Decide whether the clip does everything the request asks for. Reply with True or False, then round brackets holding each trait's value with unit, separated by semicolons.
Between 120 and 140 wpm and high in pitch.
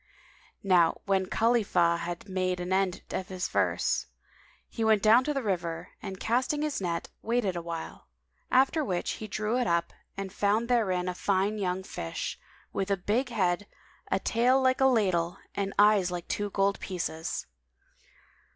False (165 wpm; 195 Hz)